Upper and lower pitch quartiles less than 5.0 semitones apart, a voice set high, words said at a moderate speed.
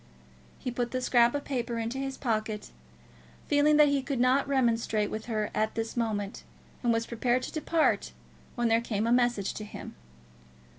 Yes: average, 2.8 semitones; high, 240 Hz; average, 180 wpm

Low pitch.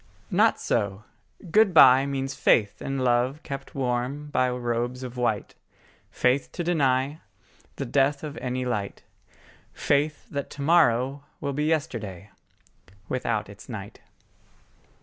Yes: low, 130 Hz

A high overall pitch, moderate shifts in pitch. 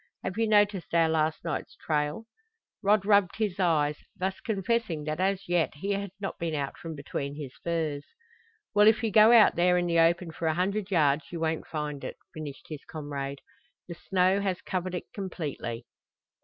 No: medium, 170 Hz; average, 4.4 semitones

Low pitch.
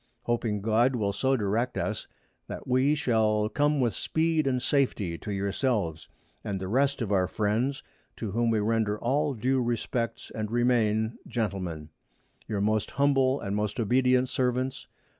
Yes: low, 115 Hz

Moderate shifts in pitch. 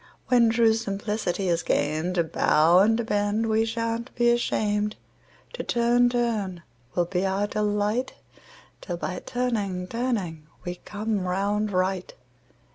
Yes: average, 3.9 semitones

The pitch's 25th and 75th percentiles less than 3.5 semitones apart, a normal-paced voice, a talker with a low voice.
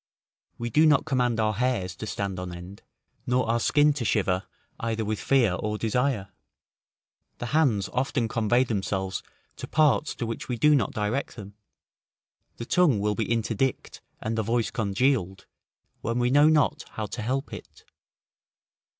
No: average, 3.9 semitones; average, 160 wpm; low, 115 Hz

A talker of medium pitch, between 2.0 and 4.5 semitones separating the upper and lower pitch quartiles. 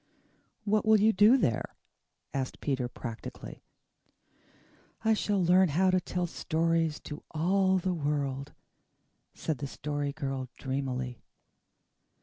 No: medium, 160 Hz; wide, 5.4 semitones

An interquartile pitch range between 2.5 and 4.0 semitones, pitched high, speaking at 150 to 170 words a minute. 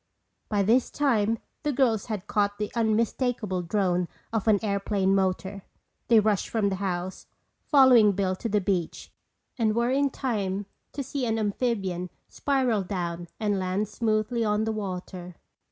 Yes: average, 3.2 semitones; high, 210 Hz; average, 155 wpm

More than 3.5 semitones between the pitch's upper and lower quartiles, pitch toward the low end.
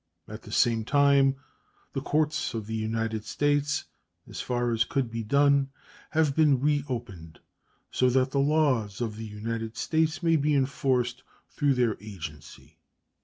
Yes: average, 4.3 semitones; low, 125 Hz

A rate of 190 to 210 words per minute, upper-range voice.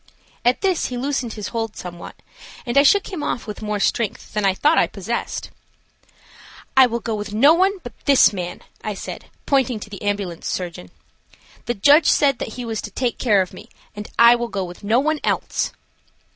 Yes: average, 200 wpm; high, 230 Hz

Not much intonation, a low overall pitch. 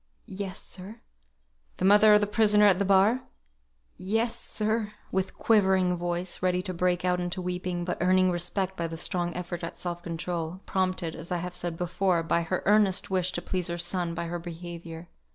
No: narrow, 1.7 semitones; medium, 180 Hz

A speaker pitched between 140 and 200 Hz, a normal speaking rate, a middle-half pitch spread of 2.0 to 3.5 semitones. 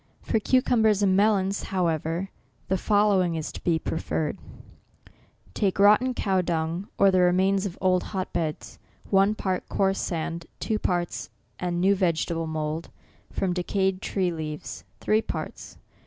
Yes: medium, 185 Hz; average, 145 wpm; average, 2.8 semitones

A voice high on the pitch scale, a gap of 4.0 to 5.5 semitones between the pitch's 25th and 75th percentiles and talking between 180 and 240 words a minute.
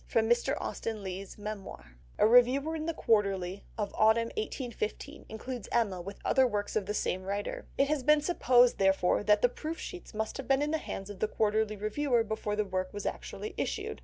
Yes: high, 220 Hz; average, 4.7 semitones; average, 200 wpm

